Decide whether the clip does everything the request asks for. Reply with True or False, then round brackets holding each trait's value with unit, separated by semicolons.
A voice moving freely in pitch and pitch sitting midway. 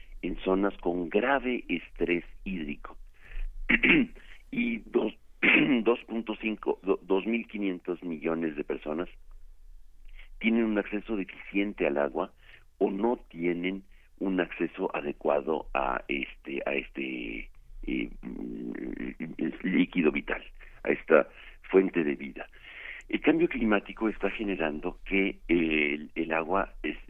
False (5.9 semitones; 90 Hz)